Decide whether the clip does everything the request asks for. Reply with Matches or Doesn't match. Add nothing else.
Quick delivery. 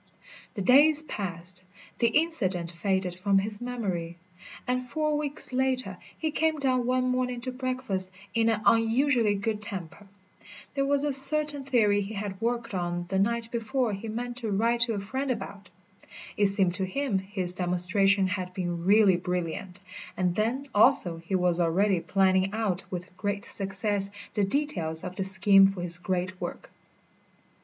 Doesn't match